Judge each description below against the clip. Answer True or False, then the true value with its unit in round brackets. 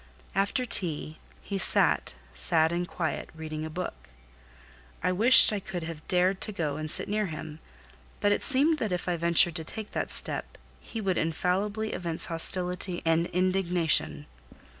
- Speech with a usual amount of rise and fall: True (3.5 semitones)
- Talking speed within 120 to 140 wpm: False (160 wpm)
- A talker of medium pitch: True (180 Hz)